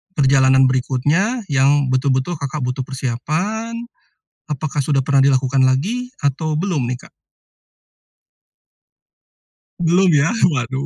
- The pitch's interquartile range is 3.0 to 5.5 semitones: Yes, average, 3.3 semitones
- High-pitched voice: No, medium, 140 Hz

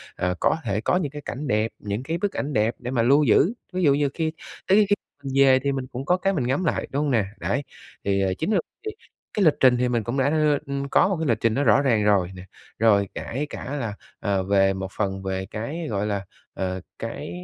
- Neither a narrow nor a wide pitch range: No, wide, 6.2 semitones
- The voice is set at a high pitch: No, low, 125 Hz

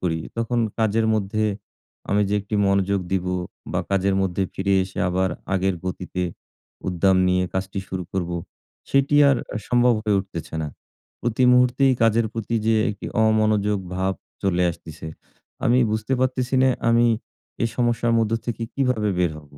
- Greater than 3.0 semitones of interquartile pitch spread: Yes, average, 3.6 semitones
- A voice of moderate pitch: No, low, 105 Hz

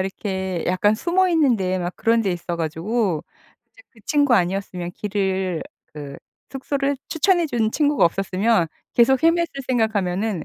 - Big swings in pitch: Yes, wide, 6.5 semitones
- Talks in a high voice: Yes, high, 210 Hz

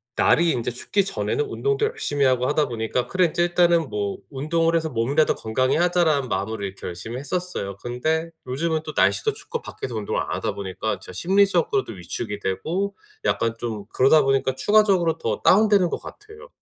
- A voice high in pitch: No, medium, 145 Hz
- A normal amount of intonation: No, wide, 7.4 semitones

